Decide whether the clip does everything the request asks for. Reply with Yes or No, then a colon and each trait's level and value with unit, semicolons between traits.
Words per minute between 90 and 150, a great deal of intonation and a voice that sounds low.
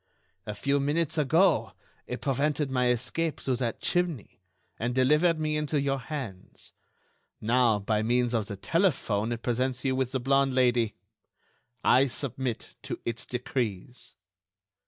No: average, 140 wpm; average, 3.4 semitones; low, 130 Hz